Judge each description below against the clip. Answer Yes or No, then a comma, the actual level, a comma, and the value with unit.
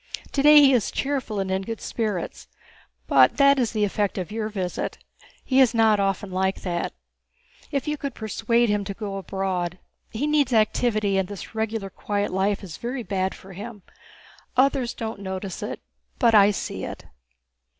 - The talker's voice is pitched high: Yes, high, 210 Hz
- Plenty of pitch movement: No, average, 3.7 semitones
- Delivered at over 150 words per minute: Yes, average, 170 wpm